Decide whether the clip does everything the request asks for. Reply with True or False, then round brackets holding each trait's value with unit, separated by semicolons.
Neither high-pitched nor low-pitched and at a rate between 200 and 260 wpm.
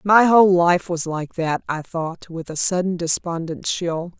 False (175 Hz; 185 wpm)